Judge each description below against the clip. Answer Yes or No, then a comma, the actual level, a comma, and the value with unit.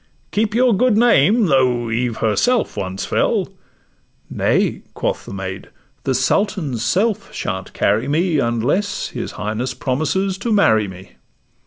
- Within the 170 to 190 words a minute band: No, slow, 135 wpm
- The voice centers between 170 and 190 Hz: No, low, 135 Hz